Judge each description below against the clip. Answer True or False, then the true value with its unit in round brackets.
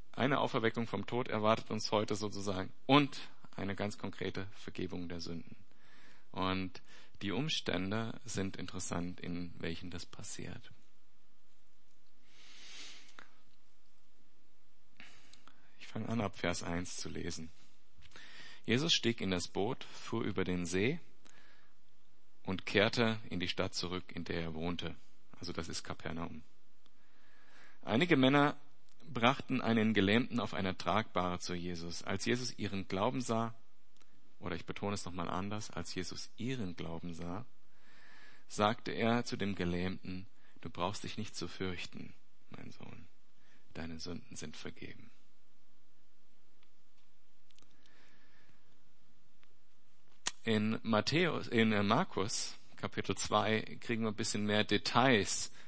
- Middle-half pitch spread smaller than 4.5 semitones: True (4.1 semitones)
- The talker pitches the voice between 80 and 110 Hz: True (100 Hz)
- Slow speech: True (120 wpm)